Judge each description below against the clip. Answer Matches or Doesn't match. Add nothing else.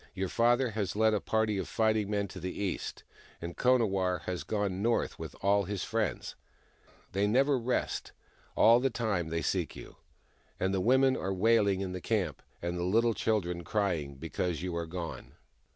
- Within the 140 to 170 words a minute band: Doesn't match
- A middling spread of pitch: Matches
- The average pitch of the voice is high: Doesn't match